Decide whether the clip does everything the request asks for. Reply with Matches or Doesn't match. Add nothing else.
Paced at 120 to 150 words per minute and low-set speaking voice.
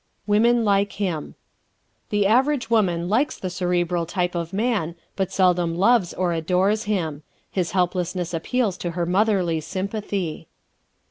Doesn't match